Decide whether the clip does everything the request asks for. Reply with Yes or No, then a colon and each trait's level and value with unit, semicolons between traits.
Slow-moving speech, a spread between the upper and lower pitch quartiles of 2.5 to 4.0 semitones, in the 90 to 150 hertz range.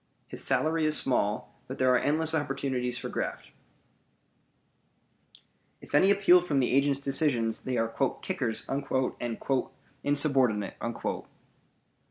Yes: slow, 115 wpm; average, 3.4 semitones; low, 135 Hz